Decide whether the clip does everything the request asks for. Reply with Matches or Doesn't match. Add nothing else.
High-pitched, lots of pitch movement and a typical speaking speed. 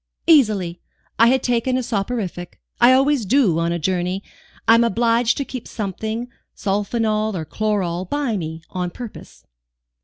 Doesn't match